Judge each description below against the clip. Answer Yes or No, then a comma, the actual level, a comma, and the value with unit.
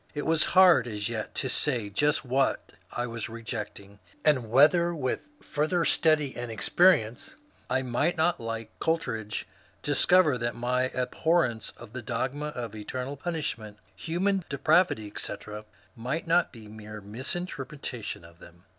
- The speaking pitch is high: No, low, 125 Hz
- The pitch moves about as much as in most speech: No, wide, 5.9 semitones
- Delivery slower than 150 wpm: Yes, average, 140 wpm